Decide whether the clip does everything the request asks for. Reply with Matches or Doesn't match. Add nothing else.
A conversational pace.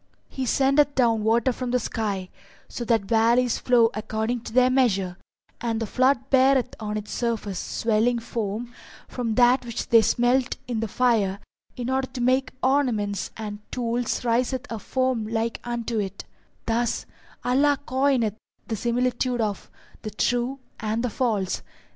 Matches